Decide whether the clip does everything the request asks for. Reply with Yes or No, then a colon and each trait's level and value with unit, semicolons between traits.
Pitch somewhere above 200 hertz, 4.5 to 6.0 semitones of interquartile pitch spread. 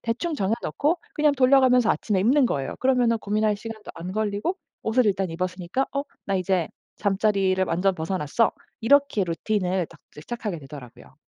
Yes: high, 210 Hz; average, 5.1 semitones